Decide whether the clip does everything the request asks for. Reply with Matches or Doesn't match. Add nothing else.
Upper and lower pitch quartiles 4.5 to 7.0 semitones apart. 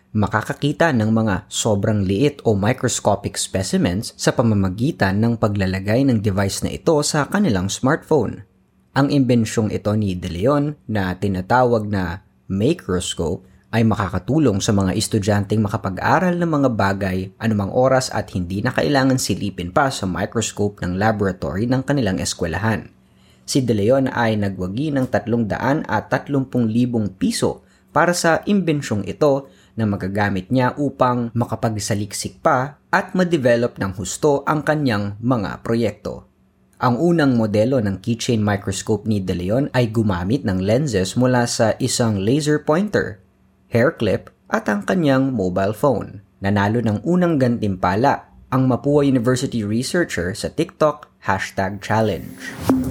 Matches